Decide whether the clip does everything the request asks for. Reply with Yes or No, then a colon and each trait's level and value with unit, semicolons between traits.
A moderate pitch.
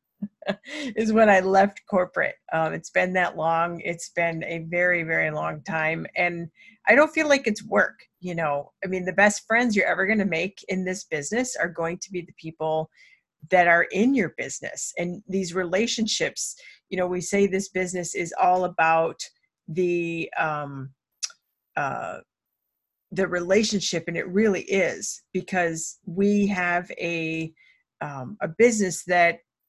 Yes: medium, 180 Hz